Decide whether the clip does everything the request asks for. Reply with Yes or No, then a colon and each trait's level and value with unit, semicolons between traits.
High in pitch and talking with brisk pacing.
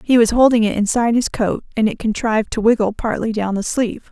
Yes: high, 225 Hz; fast, 235 wpm